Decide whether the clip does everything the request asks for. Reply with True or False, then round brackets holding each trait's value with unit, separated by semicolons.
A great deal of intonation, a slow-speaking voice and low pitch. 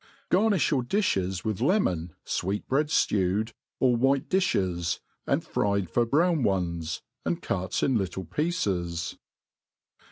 True (8.4 semitones; 115 wpm; 110 Hz)